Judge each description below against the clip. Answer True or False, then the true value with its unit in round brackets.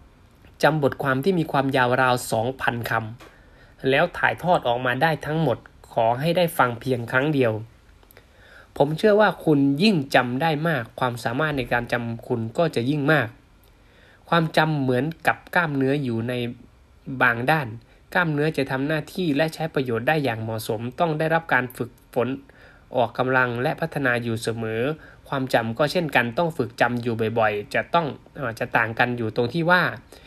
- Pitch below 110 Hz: False (130 Hz)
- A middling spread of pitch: True (4.6 semitones)